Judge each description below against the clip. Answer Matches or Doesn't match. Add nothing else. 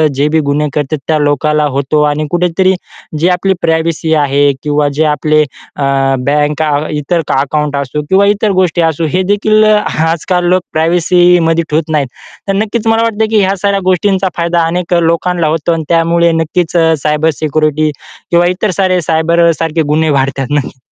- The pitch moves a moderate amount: Matches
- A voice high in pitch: Doesn't match